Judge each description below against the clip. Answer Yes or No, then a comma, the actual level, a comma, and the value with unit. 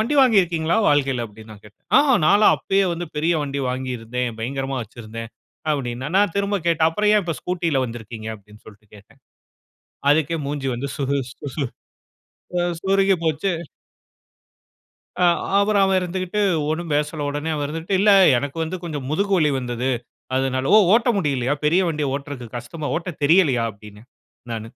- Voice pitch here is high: No, medium, 145 Hz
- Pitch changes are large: Yes, wide, 5.9 semitones